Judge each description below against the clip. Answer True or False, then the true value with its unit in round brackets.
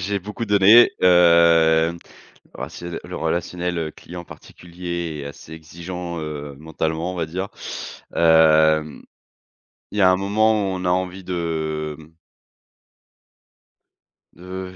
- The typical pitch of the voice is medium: False (85 Hz)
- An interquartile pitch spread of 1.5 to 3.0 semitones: True (2.5 semitones)